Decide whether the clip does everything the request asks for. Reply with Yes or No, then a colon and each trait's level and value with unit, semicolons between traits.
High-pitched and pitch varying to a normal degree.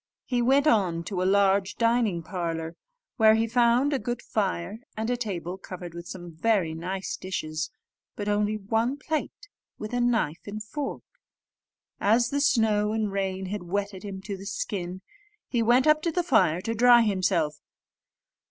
Yes: high, 205 Hz; average, 4.2 semitones